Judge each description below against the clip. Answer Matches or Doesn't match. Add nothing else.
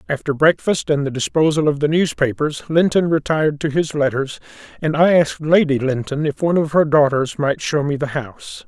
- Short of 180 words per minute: Doesn't match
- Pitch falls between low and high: Matches